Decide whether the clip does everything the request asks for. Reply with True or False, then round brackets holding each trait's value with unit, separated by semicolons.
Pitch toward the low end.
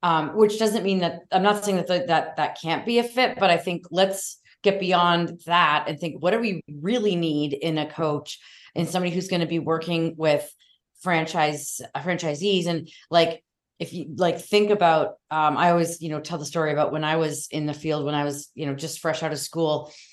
False (165 Hz)